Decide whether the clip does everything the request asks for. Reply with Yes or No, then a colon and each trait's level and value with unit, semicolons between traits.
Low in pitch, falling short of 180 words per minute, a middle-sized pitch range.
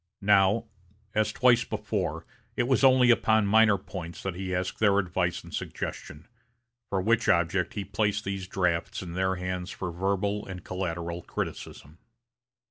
Yes: very low, 95 Hz; average, 150 wpm; average, 3.1 semitones